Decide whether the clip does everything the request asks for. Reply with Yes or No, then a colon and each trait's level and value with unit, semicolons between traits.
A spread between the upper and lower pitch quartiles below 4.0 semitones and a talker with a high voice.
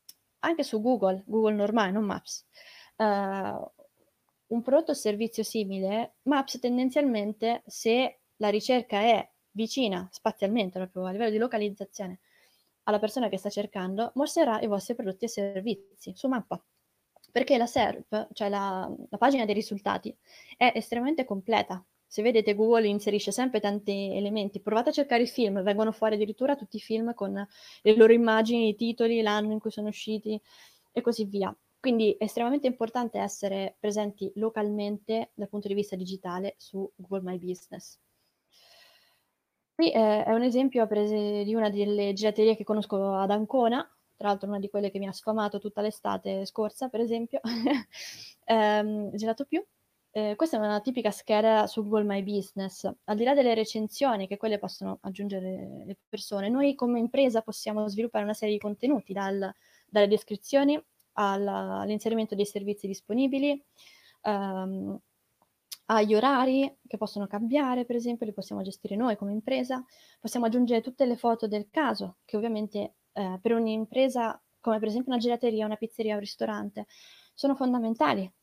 Yes: average, 2.7 semitones; high, 215 Hz